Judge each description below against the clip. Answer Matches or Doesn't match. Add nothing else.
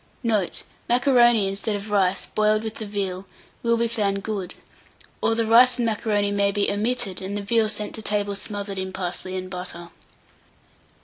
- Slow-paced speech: Doesn't match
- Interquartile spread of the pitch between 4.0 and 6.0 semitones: Doesn't match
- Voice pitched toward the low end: Doesn't match